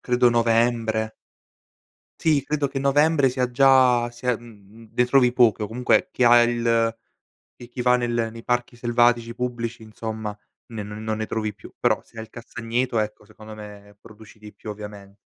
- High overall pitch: No, low, 115 Hz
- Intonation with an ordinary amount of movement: No, narrow, 2.1 semitones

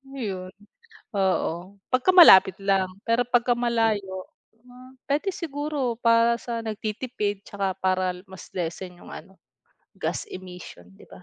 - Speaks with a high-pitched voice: Yes, high, 215 Hz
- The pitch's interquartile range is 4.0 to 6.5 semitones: Yes, average, 4.6 semitones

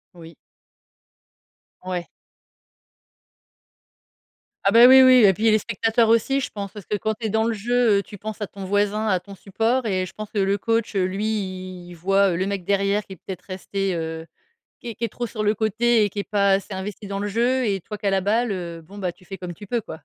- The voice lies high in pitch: Yes, high, 205 Hz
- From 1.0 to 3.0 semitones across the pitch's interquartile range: Yes, narrow, 2.6 semitones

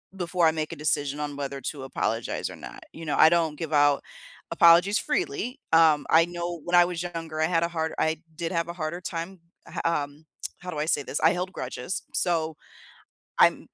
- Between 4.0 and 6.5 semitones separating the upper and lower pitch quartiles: No, narrow, 2.5 semitones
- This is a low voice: No, medium, 165 Hz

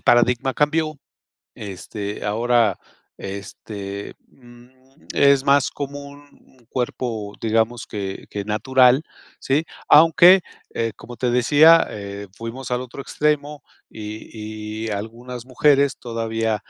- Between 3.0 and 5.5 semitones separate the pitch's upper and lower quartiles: Yes, average, 4.4 semitones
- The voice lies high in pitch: No, low, 120 Hz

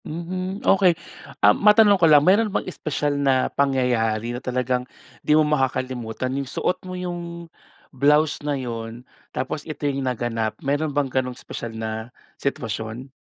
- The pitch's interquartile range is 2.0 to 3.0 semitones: No, average, 4.3 semitones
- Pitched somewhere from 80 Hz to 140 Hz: Yes, low, 135 Hz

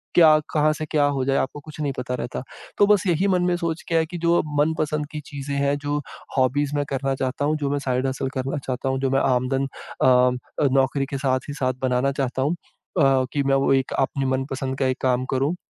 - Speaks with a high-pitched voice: No, low, 135 Hz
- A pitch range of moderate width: No, narrow, 2.3 semitones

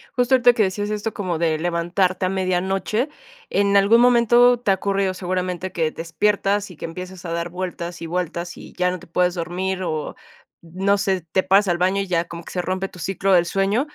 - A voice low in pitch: No, medium, 185 Hz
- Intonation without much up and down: Yes, narrow, 2.3 semitones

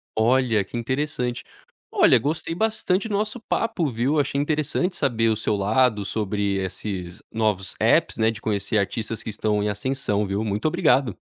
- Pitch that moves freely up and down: Yes, wide, 5.8 semitones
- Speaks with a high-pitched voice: No, low, 115 Hz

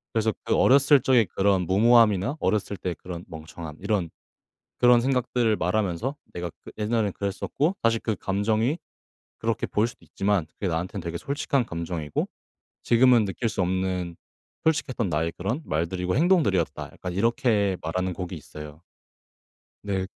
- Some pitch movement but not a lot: Yes, average, 4.8 semitones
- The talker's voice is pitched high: No, low, 100 Hz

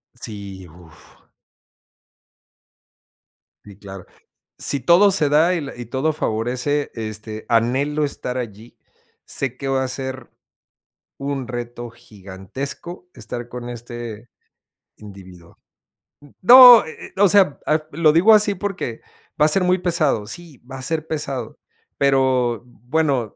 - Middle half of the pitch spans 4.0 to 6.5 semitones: Yes, wide, 5.4 semitones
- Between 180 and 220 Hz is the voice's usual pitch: No, low, 130 Hz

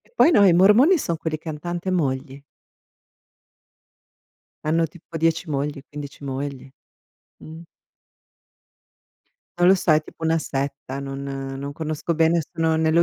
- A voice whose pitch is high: No, medium, 160 Hz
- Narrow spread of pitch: No, average, 3.2 semitones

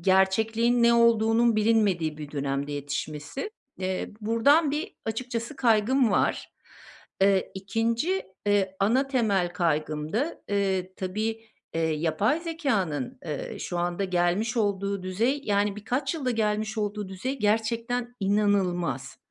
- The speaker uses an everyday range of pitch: Yes, average, 4.1 semitones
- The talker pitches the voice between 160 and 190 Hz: No, high, 210 Hz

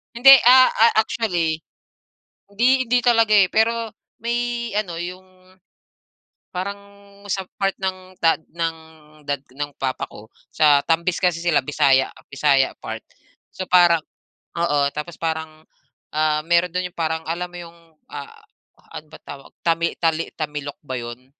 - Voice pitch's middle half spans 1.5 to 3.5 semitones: No, average, 4.2 semitones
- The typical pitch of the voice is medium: Yes, medium, 170 Hz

